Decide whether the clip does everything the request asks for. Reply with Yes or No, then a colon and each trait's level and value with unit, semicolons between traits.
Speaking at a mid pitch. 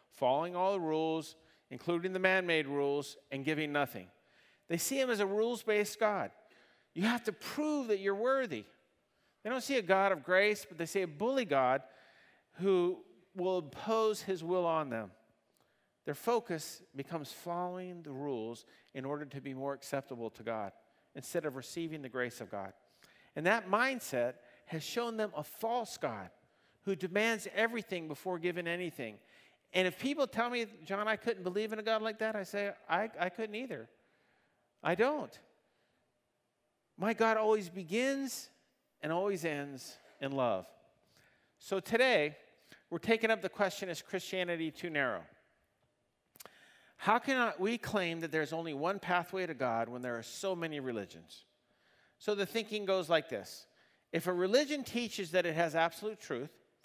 Yes: medium, 180 Hz